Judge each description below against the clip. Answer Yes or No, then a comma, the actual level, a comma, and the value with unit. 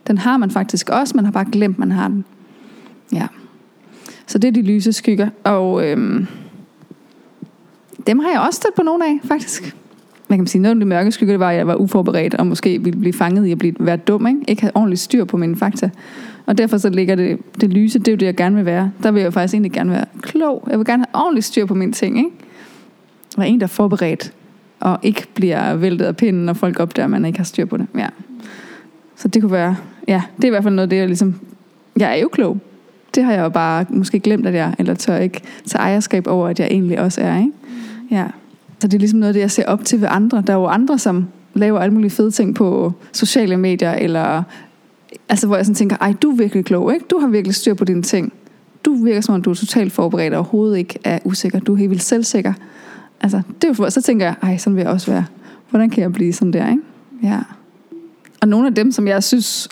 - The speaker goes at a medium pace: No, fast, 250 wpm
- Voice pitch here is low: No, high, 210 Hz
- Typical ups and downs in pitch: Yes, average, 3.7 semitones